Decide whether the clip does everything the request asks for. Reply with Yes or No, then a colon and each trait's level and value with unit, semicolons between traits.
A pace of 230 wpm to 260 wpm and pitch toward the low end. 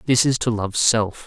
Yes: fast, 240 wpm; low, 115 Hz